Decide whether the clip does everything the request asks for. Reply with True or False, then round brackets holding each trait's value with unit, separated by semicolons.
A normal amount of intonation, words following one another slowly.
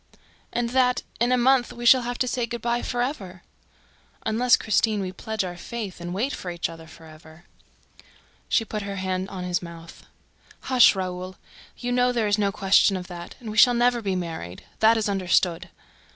False (4.9 semitones; 195 wpm)